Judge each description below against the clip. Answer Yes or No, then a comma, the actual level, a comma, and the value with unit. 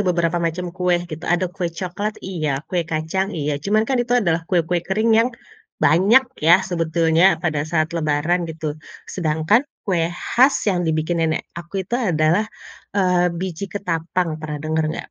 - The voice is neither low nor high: Yes, medium, 175 Hz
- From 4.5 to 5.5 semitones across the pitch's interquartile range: No, average, 2.9 semitones